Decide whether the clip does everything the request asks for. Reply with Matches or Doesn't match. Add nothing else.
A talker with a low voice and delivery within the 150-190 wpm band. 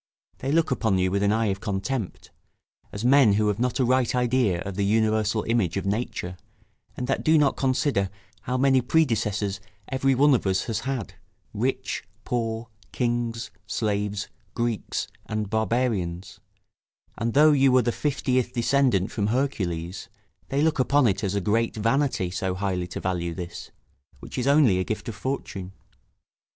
Matches